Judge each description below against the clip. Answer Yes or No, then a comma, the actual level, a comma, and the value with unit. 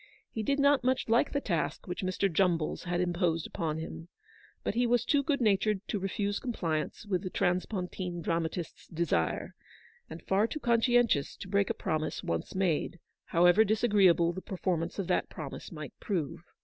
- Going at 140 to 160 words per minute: No, average, 175 wpm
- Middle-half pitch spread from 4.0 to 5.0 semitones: Yes, average, 4.5 semitones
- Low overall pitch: No, medium, 185 Hz